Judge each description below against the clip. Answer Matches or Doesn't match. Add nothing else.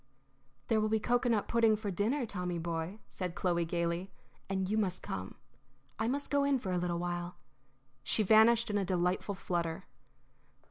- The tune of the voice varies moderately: Matches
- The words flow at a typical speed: Matches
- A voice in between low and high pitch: Doesn't match